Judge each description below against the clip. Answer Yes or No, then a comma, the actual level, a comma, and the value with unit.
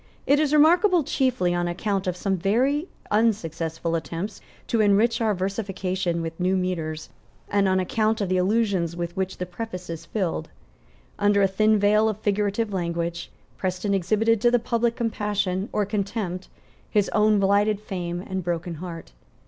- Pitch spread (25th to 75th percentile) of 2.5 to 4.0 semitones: Yes, average, 3.4 semitones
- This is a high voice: Yes, high, 195 Hz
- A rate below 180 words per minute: Yes, average, 160 wpm